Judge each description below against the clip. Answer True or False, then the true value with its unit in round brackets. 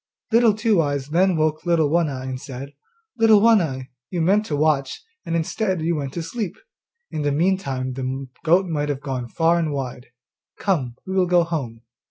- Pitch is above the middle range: False (160 Hz)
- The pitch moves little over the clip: False (5.0 semitones)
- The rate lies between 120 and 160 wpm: False (195 wpm)